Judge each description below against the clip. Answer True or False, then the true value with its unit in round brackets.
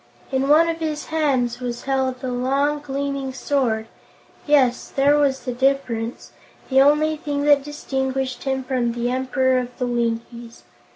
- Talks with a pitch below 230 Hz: False (265 Hz)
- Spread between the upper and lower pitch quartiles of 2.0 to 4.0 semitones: True (2.4 semitones)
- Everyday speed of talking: True (155 wpm)